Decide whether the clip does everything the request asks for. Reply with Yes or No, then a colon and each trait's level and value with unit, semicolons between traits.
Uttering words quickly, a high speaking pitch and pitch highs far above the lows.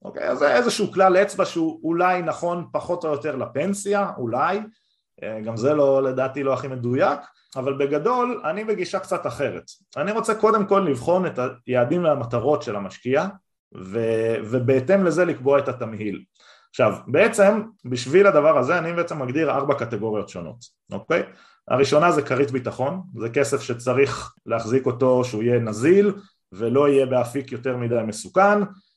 No: fast, 155 wpm; medium, 140 Hz; wide, 7.1 semitones